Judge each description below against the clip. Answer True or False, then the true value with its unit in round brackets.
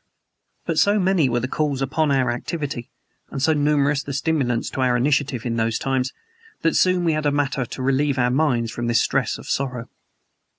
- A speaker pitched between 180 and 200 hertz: False (135 Hz)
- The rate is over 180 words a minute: True (195 wpm)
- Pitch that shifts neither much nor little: True (3.4 semitones)